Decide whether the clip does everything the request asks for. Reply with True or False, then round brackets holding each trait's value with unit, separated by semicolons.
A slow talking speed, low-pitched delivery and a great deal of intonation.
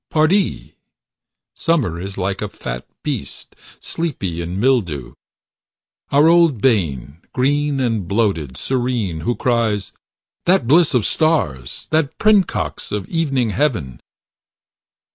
True (110 wpm; 115 Hz; 8.6 semitones)